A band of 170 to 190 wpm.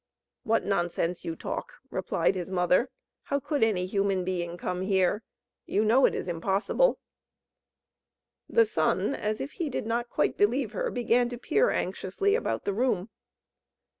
No: average, 155 wpm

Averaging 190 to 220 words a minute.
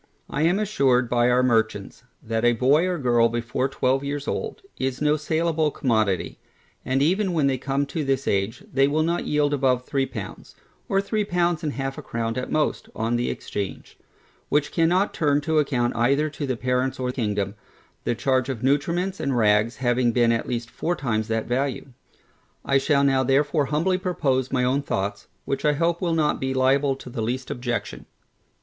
Yes: average, 195 wpm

